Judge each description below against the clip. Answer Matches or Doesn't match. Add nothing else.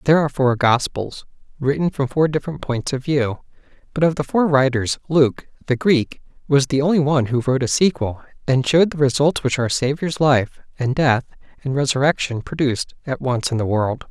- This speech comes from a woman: Doesn't match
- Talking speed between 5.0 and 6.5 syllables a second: Matches